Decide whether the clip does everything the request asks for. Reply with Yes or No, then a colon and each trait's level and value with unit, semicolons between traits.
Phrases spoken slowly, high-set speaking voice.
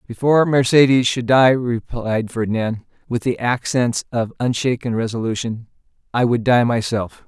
No: slow, 130 wpm; low, 120 Hz